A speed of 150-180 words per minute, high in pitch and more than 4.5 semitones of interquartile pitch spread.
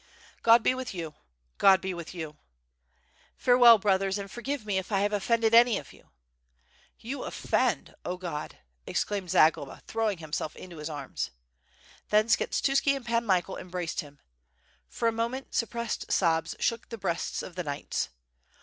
Yes: average, 160 wpm; high, 200 Hz; average, 5.1 semitones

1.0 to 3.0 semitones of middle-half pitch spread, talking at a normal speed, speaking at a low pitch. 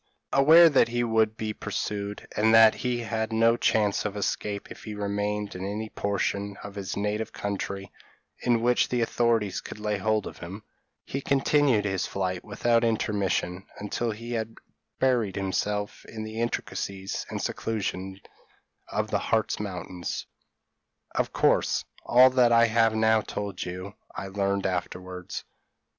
Yes: narrow, 2.5 semitones; average, 150 wpm; low, 105 Hz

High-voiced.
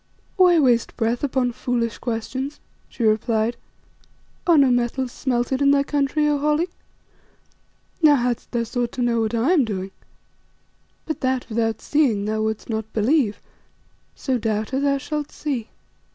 Yes: high, 245 Hz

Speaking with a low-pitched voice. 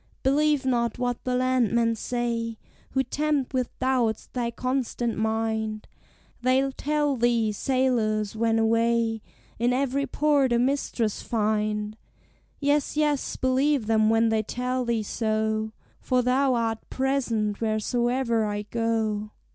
No: high, 235 Hz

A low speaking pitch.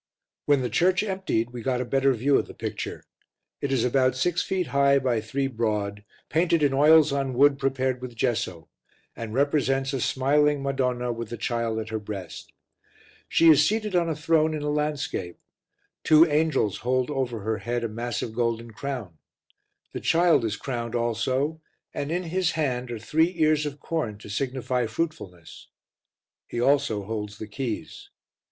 Yes: low, 130 Hz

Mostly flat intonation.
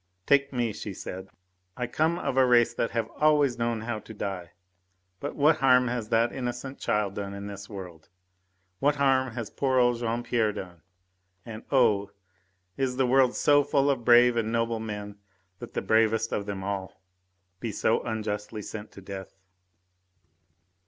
No: average, 3.6 semitones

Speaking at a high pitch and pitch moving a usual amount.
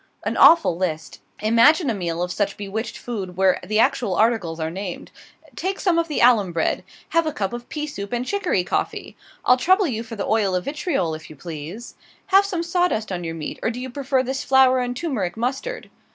No: high, 230 Hz; wide, 7.2 semitones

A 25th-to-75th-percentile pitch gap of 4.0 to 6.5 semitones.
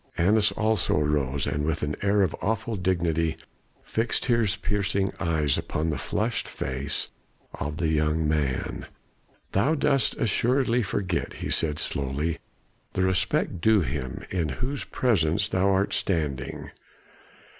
Yes: wide, 5.5 semitones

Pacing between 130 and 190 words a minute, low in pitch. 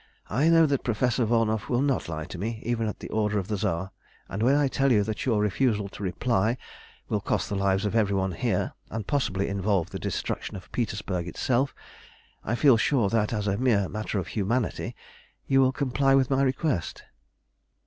No: average, 200 wpm; low, 110 Hz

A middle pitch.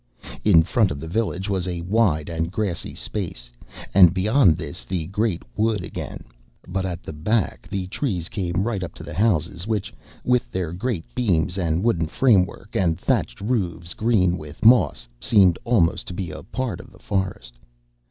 No: very low, 95 Hz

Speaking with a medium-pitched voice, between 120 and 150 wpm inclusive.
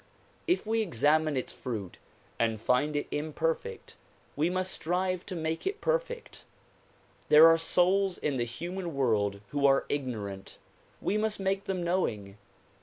Yes: medium, 160 Hz; average, 145 wpm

